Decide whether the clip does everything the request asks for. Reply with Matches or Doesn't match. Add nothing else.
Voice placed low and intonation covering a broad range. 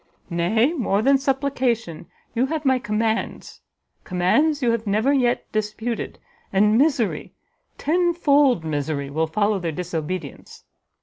Doesn't match